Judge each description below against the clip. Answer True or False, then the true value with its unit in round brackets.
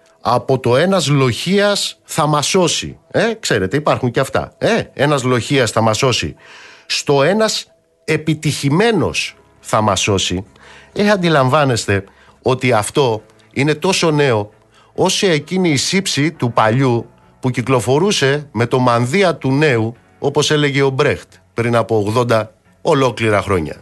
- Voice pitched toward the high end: False (135 Hz)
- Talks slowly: False (135 wpm)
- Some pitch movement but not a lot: False (5.8 semitones)